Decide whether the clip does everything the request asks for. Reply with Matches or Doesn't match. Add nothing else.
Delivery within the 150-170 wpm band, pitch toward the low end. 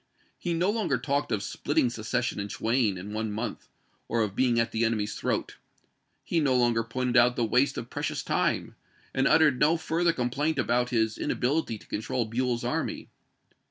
Doesn't match